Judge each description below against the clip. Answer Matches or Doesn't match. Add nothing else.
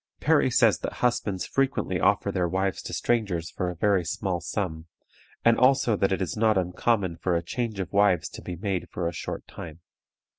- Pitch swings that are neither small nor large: Matches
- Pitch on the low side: Matches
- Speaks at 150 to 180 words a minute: Doesn't match